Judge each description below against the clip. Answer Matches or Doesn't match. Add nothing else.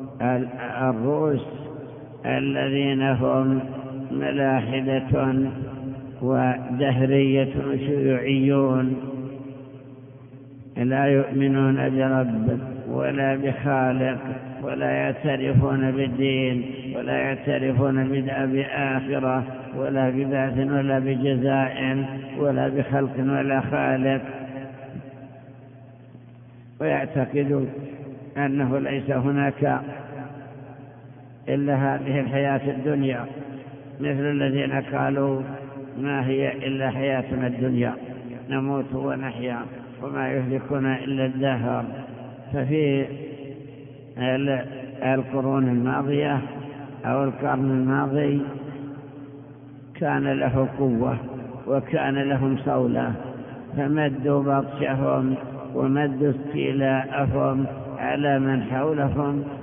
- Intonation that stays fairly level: Matches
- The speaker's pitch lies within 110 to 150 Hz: Matches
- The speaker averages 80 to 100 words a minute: Doesn't match